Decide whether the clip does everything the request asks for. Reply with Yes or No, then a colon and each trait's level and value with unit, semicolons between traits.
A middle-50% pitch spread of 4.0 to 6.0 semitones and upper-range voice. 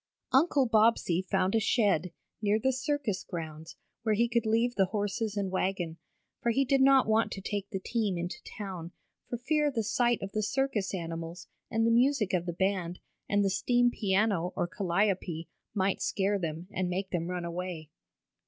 Yes: average, 4.3 semitones; high, 200 Hz